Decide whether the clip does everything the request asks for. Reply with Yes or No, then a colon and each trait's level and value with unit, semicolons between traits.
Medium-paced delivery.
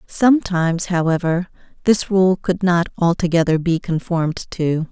No: slow, 120 wpm